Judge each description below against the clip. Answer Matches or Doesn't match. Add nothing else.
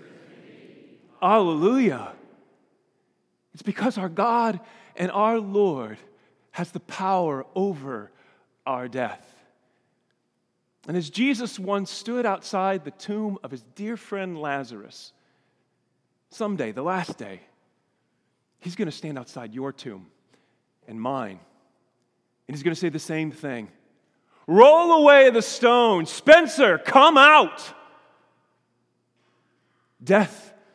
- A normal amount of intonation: Doesn't match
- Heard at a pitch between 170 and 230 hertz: Matches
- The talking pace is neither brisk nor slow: Doesn't match